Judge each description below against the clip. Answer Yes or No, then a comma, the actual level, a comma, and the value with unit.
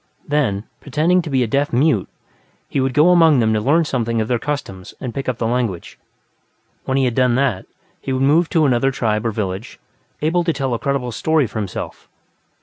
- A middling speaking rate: No, fast, 215 wpm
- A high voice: No, low, 130 Hz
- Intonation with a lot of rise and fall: No, average, 4.4 semitones